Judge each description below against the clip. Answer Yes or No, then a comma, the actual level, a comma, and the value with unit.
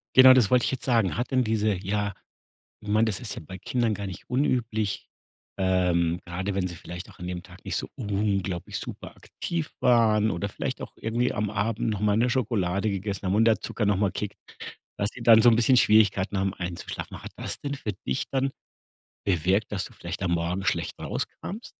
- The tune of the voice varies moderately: Yes, average, 3.6 semitones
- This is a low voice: Yes, low, 105 Hz